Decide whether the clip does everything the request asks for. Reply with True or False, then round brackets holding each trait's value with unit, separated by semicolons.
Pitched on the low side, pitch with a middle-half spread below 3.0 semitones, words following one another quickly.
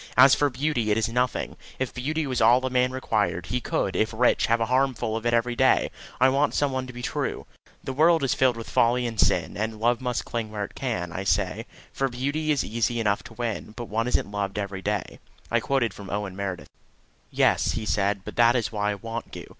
False (115 Hz; 3.3 semitones; 235 wpm)